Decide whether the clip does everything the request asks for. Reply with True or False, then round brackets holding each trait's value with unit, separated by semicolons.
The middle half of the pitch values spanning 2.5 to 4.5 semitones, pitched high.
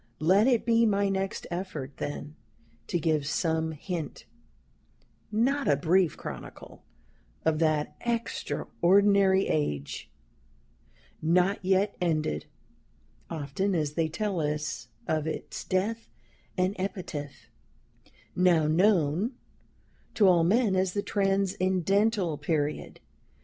False (4.2 semitones; 180 Hz)